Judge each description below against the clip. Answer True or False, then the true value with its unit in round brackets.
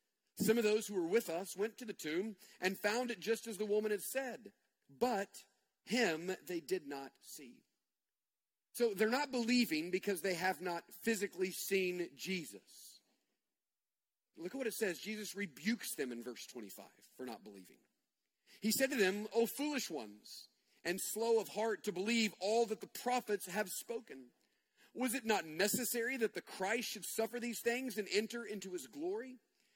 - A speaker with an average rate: True (175 wpm)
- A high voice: True (215 Hz)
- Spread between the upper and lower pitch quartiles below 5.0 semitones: True (3.9 semitones)